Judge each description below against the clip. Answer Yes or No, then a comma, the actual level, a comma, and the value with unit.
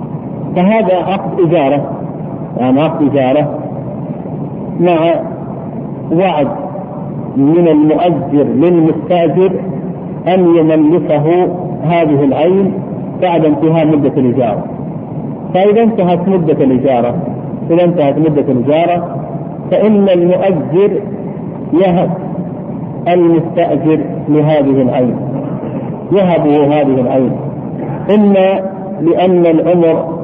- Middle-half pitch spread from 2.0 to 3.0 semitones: No, average, 3.4 semitones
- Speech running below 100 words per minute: Yes, average, 75 wpm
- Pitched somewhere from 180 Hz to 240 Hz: No, medium, 170 Hz